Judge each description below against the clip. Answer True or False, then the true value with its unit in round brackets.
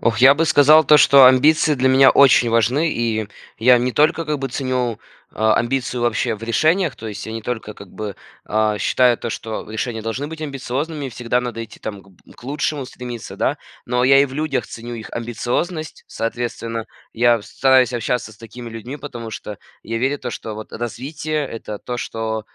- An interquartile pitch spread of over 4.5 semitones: False (3.4 semitones)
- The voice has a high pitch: False (120 Hz)